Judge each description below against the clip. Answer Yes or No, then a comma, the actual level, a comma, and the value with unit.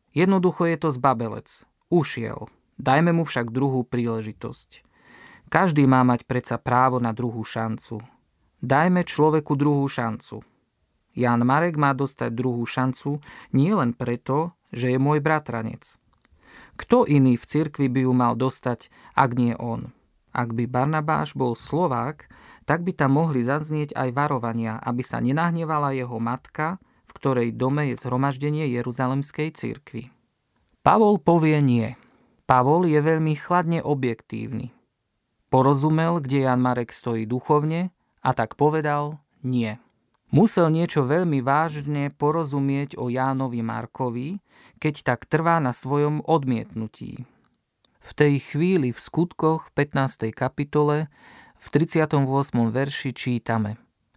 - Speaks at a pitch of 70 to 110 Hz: No, low, 135 Hz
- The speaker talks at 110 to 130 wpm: Yes, average, 125 wpm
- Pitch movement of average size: Yes, average, 4.0 semitones